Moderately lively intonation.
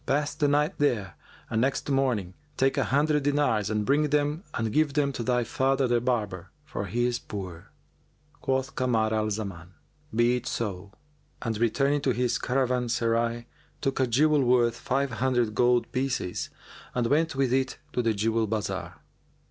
Yes: average, 3.3 semitones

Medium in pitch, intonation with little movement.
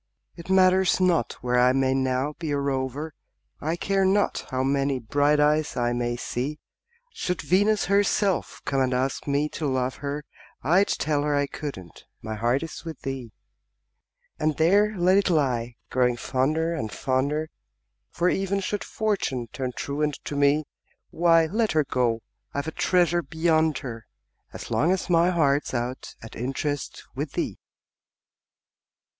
No: medium, 145 Hz; average, 4.7 semitones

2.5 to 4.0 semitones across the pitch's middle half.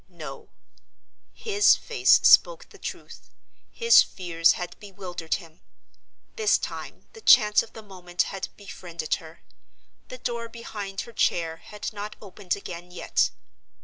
No: average, 4.6 semitones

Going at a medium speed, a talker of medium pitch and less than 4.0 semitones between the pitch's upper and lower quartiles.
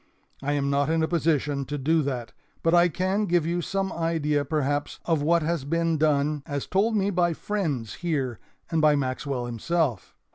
Yes: average, 185 wpm; medium, 155 Hz; average, 3.3 semitones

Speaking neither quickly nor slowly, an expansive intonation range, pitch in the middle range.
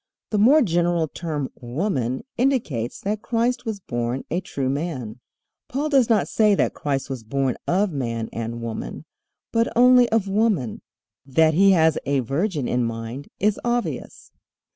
Yes: average, 155 wpm; wide, 9.0 semitones; medium, 160 Hz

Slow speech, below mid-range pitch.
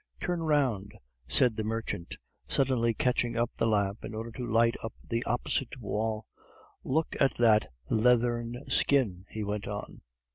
No: average, 150 wpm; low, 115 Hz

